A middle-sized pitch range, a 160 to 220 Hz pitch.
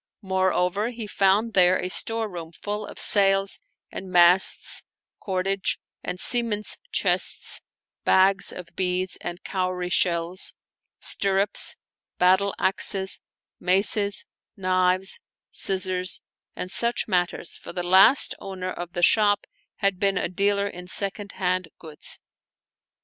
No: narrow, 1.7 semitones; high, 190 Hz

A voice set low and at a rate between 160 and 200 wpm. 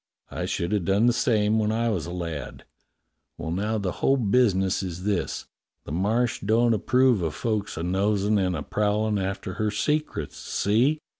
Yes: low, 105 Hz; average, 175 wpm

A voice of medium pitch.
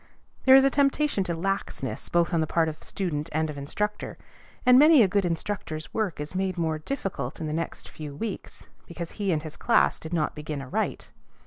Yes: medium, 170 Hz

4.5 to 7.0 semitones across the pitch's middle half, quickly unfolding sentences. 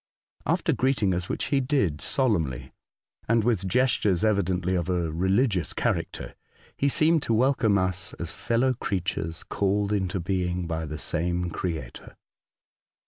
No: average, 4.9 semitones; average, 140 wpm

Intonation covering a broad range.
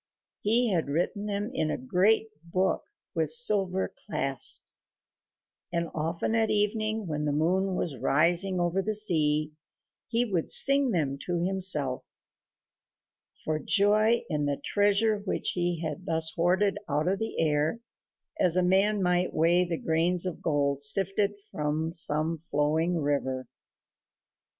No: average, 4.6 semitones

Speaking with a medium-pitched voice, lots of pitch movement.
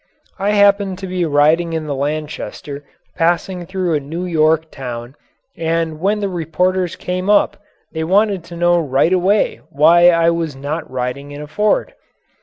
No: medium, 165 Hz; average, 3.4 semitones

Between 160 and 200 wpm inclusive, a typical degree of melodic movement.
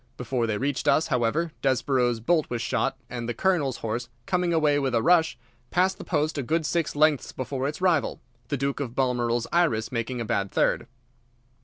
Yes: average, 190 wpm; average, 4.9 semitones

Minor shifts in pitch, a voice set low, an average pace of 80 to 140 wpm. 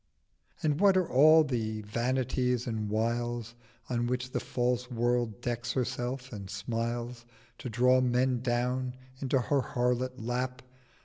Yes: narrow, 1.4 semitones; low, 125 Hz; slow, 135 wpm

